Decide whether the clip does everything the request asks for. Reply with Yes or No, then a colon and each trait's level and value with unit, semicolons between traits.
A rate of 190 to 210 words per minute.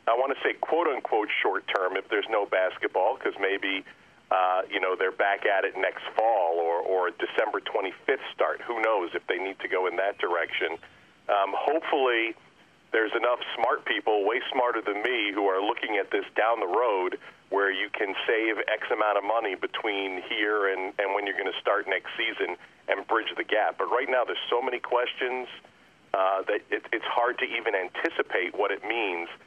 Yes: average, 200 wpm